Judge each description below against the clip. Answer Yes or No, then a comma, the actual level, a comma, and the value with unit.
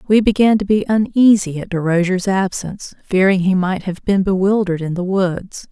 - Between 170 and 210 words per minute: Yes, average, 180 wpm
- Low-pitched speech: No, high, 190 Hz